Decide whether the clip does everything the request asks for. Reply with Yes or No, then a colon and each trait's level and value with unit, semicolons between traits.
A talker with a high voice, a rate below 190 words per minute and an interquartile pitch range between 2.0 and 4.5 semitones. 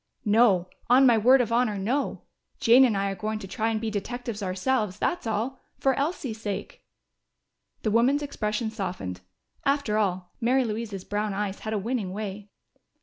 Yes: high, 220 Hz; average, 170 wpm; average, 3.4 semitones